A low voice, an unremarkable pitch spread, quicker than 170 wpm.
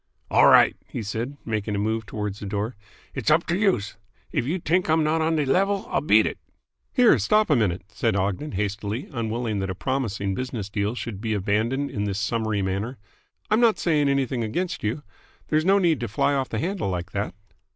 No: low, 115 Hz; wide, 7.0 semitones; fast, 205 wpm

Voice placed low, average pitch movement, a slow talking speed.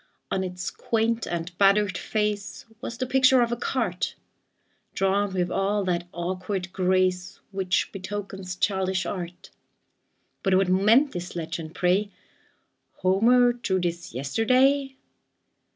No: high, 190 Hz; average, 3.6 semitones; slow, 120 wpm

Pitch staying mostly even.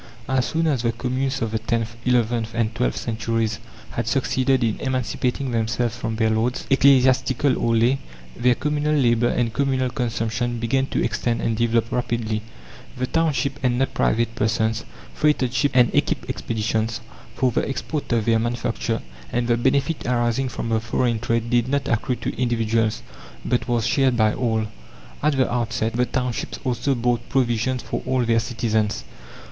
Yes: narrow, 2.2 semitones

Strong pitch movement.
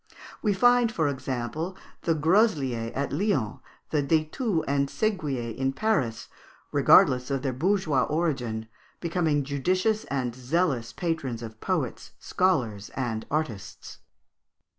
Yes: wide, 6.1 semitones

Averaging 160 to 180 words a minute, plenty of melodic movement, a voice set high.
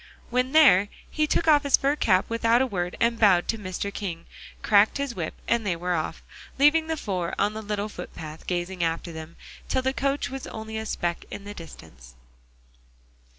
No: average, 195 wpm; wide, 6.7 semitones; high, 210 Hz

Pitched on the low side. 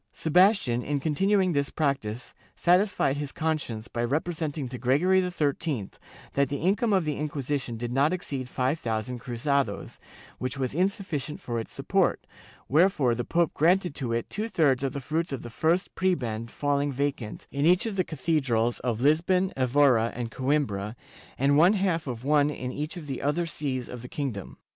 No: medium, 145 Hz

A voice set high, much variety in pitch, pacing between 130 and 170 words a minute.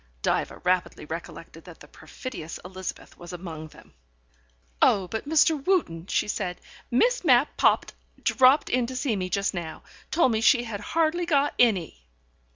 Yes: high, 210 Hz; wide, 7.8 semitones; average, 160 wpm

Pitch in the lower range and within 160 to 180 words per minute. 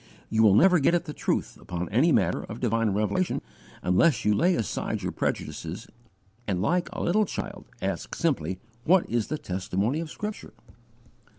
Yes: low, 120 Hz; average, 175 wpm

